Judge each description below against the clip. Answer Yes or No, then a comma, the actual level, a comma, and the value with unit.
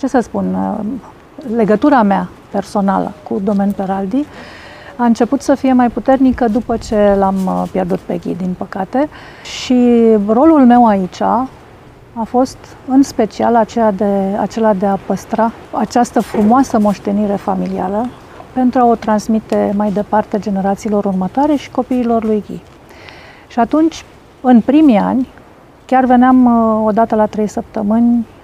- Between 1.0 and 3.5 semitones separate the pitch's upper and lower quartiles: Yes, average, 3.2 semitones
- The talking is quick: No, average, 135 wpm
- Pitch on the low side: No, high, 225 Hz